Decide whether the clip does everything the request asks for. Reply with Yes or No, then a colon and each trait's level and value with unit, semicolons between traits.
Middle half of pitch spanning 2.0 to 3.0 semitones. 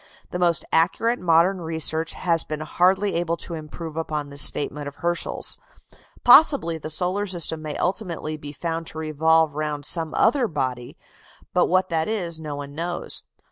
Yes: narrow, 2.6 semitones